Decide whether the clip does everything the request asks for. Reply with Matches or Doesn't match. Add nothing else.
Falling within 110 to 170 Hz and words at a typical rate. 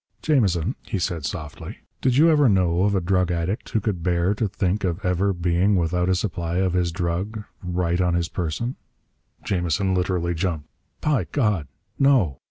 Doesn't match